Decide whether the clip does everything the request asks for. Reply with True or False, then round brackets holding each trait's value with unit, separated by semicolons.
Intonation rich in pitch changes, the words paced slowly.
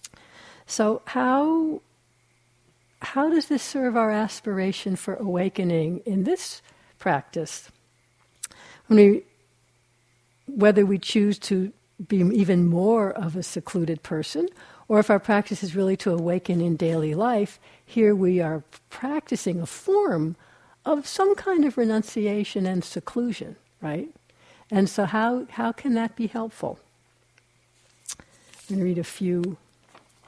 False (4.7 semitones; 130 wpm)